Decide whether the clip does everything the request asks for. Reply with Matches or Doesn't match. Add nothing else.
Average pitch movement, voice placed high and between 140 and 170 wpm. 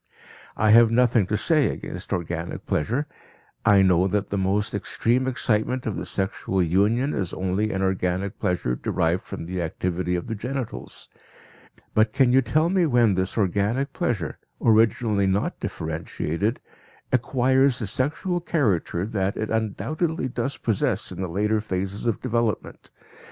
Doesn't match